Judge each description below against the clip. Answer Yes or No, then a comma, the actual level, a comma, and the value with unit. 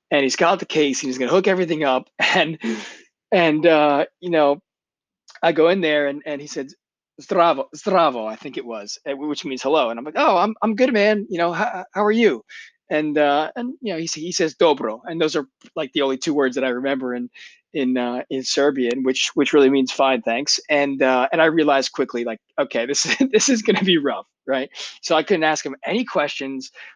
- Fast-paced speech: Yes, fast, 230 wpm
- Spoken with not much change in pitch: No, average, 4.4 semitones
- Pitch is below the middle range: No, medium, 150 Hz